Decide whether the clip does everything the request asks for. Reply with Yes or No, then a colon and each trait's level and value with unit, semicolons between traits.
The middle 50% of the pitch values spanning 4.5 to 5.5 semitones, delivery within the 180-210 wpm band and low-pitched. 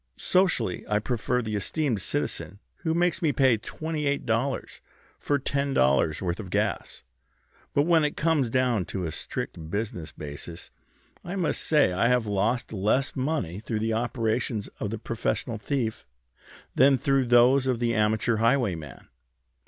No: average, 5.0 semitones; average, 155 wpm; low, 120 Hz